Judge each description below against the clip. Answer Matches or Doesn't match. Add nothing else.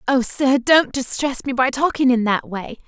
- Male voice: Doesn't match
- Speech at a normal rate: Doesn't match